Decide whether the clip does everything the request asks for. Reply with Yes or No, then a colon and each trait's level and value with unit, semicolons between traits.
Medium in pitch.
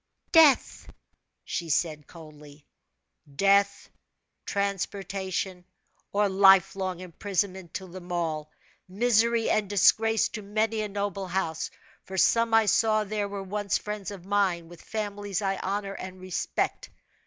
No: high, 195 Hz